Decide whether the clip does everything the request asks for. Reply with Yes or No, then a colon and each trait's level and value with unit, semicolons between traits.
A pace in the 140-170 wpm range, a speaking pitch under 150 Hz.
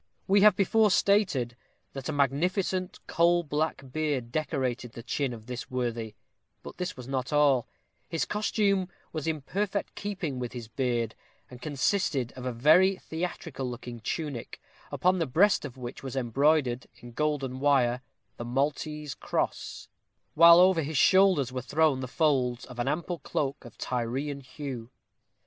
Yes: average, 155 wpm; medium, 140 Hz